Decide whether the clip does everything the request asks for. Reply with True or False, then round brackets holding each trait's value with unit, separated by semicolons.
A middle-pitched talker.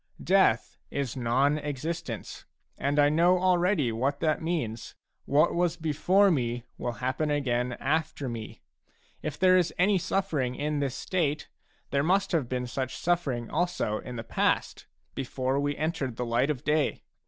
True (145 Hz)